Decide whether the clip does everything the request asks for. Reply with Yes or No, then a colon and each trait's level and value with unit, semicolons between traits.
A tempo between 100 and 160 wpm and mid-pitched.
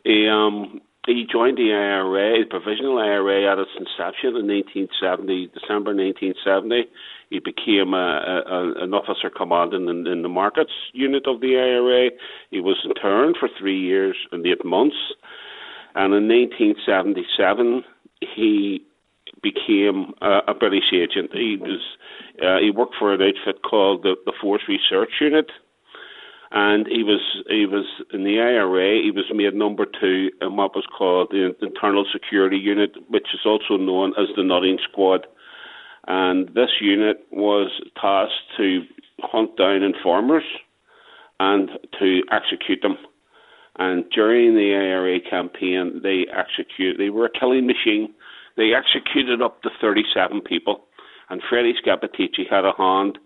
No: average, 145 wpm; low, 105 Hz